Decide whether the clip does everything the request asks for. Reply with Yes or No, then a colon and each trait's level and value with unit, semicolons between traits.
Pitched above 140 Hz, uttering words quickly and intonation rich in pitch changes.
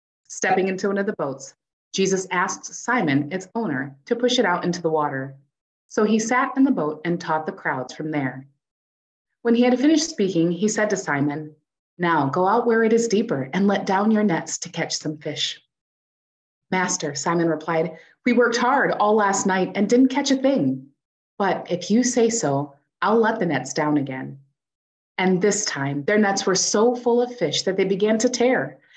No: medium, 185 Hz; average, 195 wpm; wide, 6.5 semitones